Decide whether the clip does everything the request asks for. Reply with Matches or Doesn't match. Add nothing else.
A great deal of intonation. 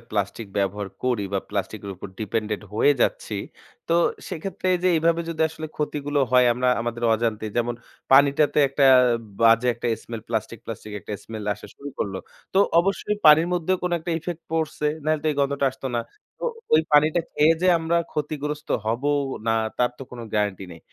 Matches